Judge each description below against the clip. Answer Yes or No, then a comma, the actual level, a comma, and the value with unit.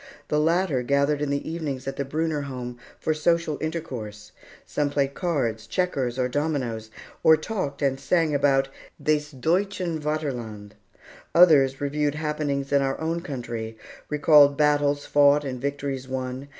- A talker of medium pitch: Yes, medium, 145 Hz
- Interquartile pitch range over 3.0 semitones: No, average, 2.7 semitones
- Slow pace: No, average, 145 wpm